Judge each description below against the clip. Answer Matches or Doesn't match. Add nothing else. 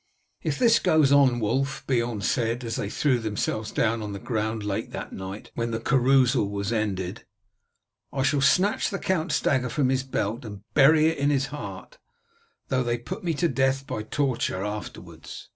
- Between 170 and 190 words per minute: Matches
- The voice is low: Matches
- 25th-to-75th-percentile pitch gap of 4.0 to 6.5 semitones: Matches